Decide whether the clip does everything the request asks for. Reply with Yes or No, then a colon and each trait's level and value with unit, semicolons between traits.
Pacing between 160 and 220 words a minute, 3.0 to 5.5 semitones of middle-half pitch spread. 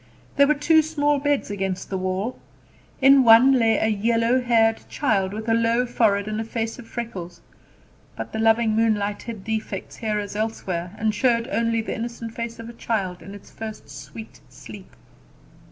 No: average, 180 wpm; narrow, 2.5 semitones